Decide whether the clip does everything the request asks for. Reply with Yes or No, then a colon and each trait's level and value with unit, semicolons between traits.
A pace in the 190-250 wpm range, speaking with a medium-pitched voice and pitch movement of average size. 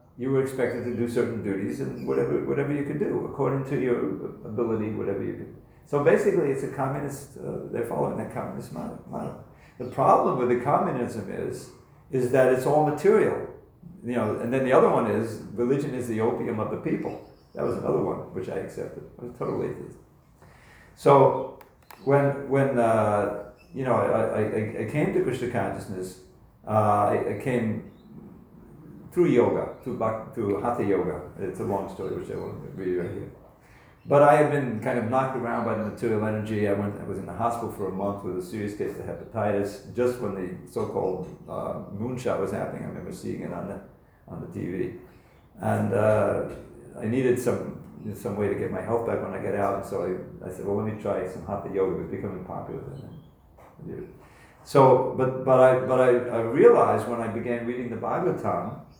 No: average, 195 wpm; low, 120 Hz; average, 4.0 semitones